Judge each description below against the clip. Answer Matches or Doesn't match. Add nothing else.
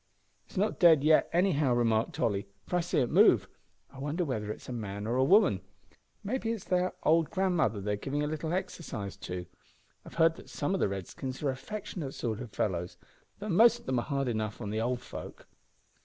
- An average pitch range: Doesn't match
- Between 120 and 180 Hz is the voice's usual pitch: Matches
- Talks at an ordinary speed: Doesn't match